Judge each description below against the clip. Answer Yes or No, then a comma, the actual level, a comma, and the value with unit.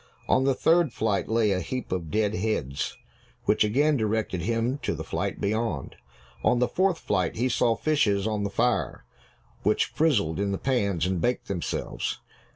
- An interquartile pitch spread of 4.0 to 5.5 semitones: Yes, average, 4.3 semitones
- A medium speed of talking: Yes, average, 170 wpm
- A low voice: Yes, low, 110 Hz